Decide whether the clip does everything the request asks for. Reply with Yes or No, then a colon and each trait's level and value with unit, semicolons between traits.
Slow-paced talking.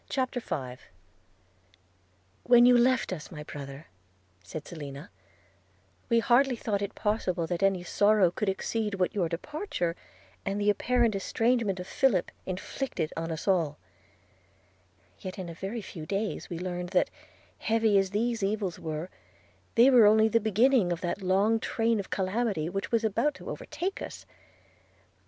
No: average, 150 wpm